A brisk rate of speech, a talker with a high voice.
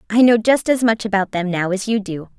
Yes: fast, 275 wpm; high, 210 Hz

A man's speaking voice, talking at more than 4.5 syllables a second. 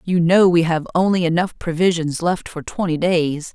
No: female; 4.7 syllables/s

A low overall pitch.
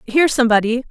No: high, 245 Hz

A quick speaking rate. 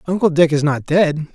Yes: fast, 225 wpm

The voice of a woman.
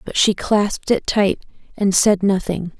Yes: female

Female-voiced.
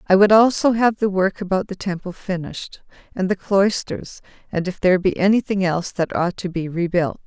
Yes: female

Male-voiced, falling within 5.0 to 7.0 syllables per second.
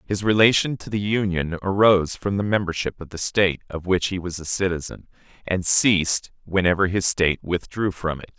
Yes: male; 5.4 syllables/s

